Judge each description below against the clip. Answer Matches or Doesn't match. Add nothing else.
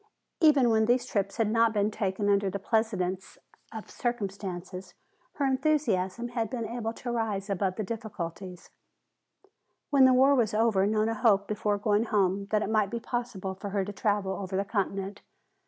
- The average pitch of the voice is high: Matches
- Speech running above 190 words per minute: Doesn't match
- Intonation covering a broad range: Doesn't match